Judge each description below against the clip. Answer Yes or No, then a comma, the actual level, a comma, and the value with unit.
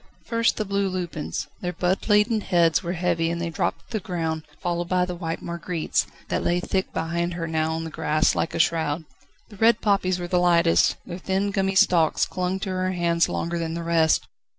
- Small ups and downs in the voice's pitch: Yes, narrow, 2.2 semitones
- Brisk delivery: Yes, fast, 210 wpm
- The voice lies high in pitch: No, medium, 175 Hz